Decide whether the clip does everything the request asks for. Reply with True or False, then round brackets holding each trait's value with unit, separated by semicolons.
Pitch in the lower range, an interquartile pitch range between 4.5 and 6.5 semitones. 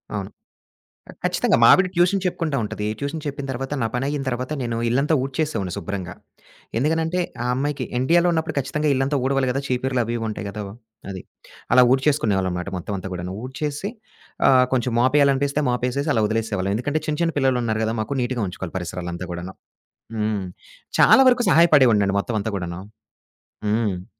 True (125 Hz; 5.6 semitones)